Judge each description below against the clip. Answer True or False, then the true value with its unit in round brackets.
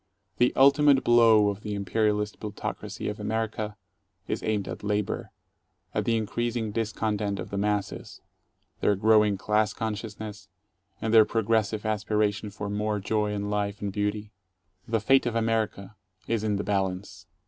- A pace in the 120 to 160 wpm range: True (150 wpm)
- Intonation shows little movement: True (1.4 semitones)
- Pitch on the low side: True (105 Hz)